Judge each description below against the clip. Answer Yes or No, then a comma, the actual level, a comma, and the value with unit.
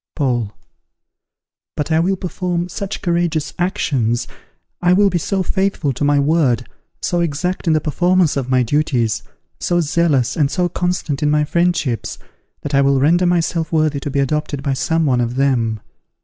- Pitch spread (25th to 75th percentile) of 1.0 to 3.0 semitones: No, average, 4.1 semitones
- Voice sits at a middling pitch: Yes, medium, 155 Hz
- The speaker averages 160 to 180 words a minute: Yes, average, 170 wpm